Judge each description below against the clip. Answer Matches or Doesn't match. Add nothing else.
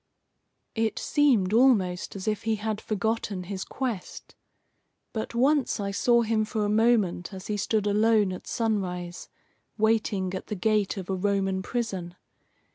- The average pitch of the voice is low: Doesn't match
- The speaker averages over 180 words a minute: Doesn't match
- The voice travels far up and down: Doesn't match